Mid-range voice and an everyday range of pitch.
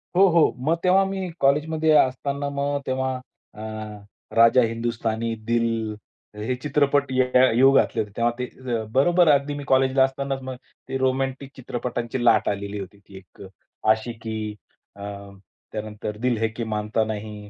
No: low, 130 Hz; average, 3.8 semitones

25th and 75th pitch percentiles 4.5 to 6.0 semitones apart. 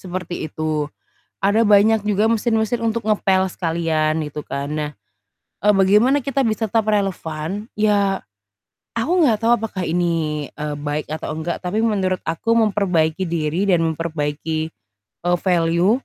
Yes: average, 5.0 semitones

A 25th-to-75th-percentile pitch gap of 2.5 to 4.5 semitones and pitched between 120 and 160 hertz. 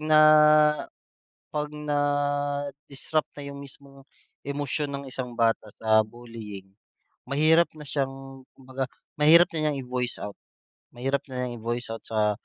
Yes: average, 3.1 semitones; low, 135 Hz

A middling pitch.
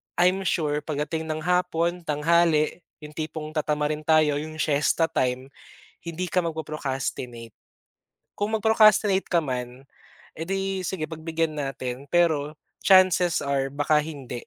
Yes: medium, 155 Hz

